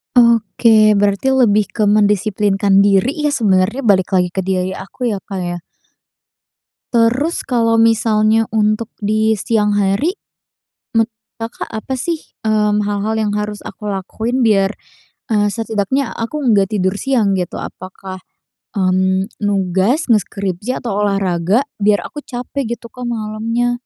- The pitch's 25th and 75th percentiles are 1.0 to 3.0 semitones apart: Yes, average, 2.7 semitones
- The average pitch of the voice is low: No, high, 210 Hz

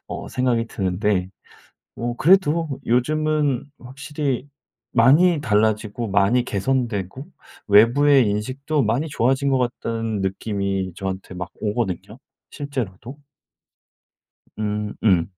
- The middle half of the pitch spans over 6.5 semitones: No, average, 5.2 semitones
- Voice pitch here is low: Yes, low, 120 Hz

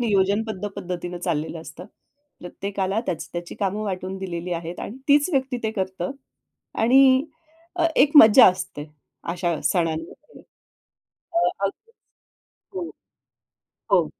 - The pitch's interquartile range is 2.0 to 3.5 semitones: No, average, 4.3 semitones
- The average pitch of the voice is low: No, high, 190 Hz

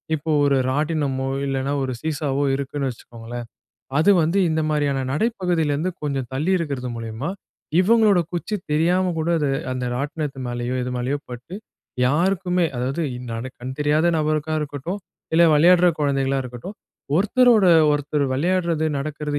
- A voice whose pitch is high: No, medium, 150 Hz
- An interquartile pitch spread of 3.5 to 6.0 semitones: Yes, average, 4.1 semitones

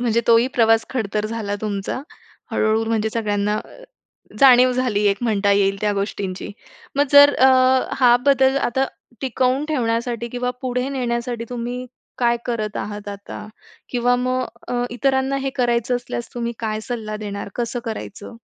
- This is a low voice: No, high, 235 Hz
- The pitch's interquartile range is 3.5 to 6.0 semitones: No, average, 2.8 semitones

